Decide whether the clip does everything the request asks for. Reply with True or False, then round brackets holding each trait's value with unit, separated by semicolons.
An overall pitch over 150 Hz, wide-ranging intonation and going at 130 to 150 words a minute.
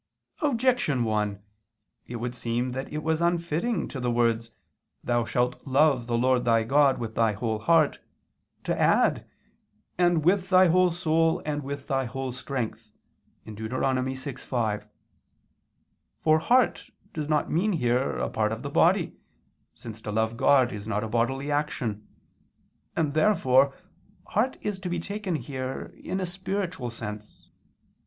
False (135 Hz; 5.9 semitones; 145 wpm)